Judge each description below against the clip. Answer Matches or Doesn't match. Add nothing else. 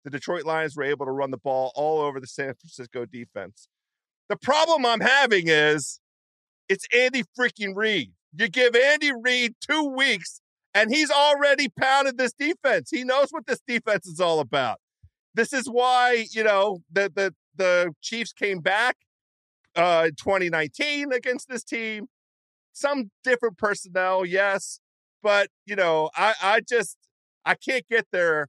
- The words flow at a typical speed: Matches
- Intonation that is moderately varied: Doesn't match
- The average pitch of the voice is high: Matches